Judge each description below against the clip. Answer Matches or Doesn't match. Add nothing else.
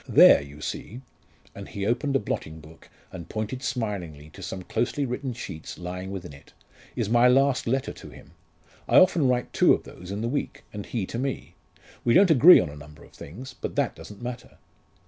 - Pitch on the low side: Matches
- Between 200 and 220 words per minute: Matches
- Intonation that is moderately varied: Doesn't match